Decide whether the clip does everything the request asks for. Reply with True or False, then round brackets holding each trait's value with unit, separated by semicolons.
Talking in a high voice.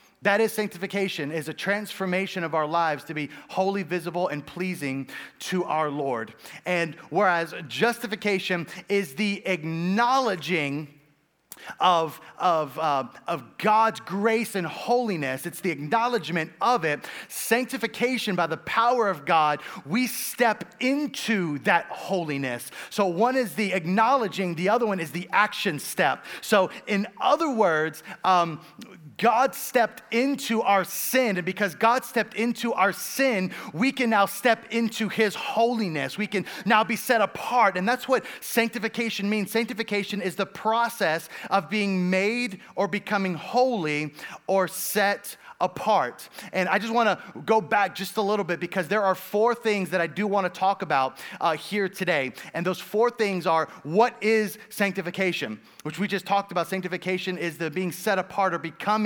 True (195 Hz)